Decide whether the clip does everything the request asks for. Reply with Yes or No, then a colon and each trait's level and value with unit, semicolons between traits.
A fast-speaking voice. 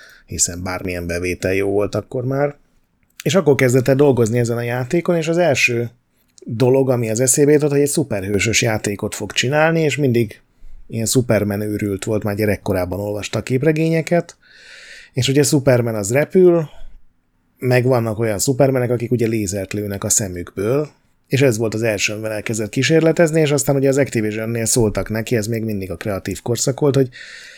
Yes: fast, 170 wpm